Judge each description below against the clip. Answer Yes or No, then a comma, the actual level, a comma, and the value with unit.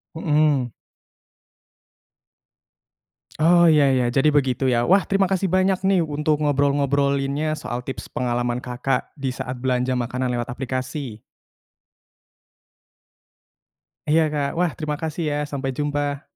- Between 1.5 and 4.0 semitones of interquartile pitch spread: Yes, average, 3.2 semitones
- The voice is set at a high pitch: No, medium, 140 Hz